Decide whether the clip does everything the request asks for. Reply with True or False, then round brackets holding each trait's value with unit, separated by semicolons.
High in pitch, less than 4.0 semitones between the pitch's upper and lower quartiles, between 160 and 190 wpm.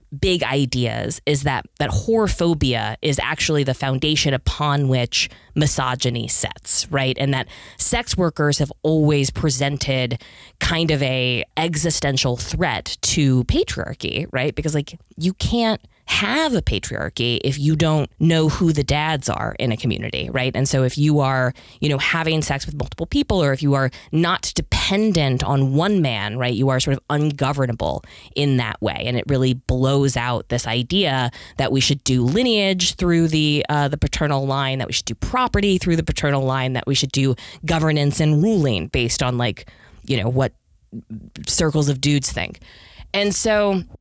False (140 Hz; 3.5 semitones; 170 wpm)